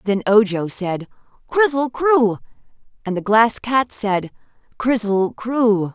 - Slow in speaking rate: Yes, slow, 120 wpm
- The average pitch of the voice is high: Yes, high, 220 Hz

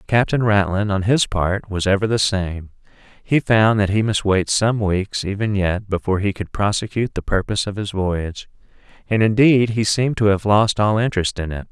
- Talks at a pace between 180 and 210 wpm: Yes, average, 200 wpm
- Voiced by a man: Yes, male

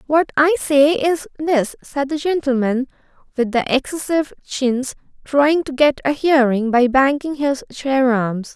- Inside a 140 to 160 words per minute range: Yes, average, 155 wpm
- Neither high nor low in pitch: No, very high, 275 Hz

